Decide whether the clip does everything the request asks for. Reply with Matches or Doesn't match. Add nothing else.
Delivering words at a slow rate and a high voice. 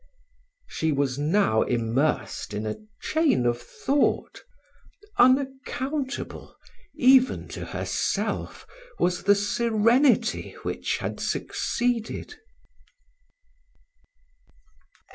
Matches